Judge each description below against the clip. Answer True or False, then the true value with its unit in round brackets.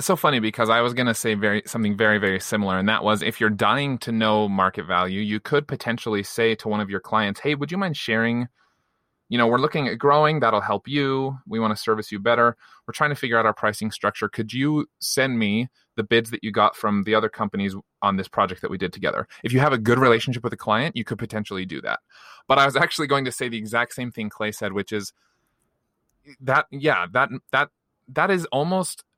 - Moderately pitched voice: False (115 Hz)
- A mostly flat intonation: False (4.0 semitones)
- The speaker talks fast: True (235 wpm)